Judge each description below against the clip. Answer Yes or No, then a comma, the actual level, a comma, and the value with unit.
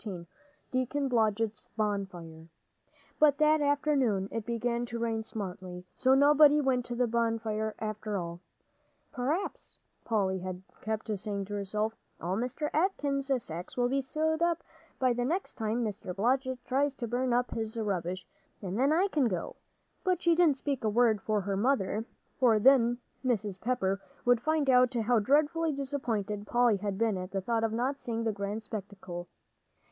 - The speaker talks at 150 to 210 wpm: Yes, average, 165 wpm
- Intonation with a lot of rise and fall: No, average, 4.7 semitones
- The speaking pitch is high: Yes, high, 230 Hz